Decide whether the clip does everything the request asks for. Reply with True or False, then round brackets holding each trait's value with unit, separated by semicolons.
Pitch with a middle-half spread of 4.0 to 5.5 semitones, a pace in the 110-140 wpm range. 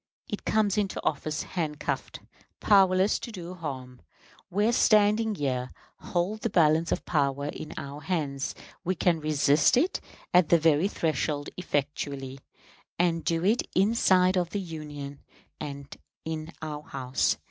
True (4.6 semitones; 135 wpm)